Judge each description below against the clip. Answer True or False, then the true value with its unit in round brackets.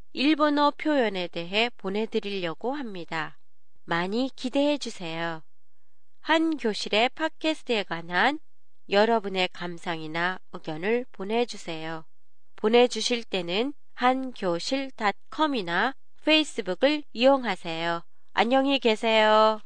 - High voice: True (220 Hz)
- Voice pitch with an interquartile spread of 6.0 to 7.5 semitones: True (6.6 semitones)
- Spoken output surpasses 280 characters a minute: False (250 characters per minute)